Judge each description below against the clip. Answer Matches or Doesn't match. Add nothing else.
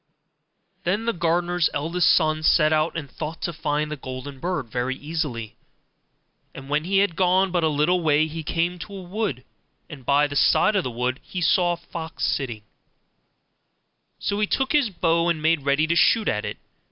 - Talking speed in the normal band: Matches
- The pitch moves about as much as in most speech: Matches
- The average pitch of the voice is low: Doesn't match